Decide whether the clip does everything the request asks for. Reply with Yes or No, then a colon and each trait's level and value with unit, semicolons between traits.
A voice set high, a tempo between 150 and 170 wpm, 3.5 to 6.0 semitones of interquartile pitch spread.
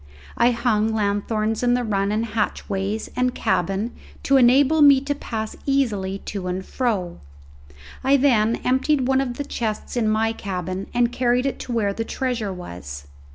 Yes: high, 225 Hz; average, 165 wpm; average, 3.8 semitones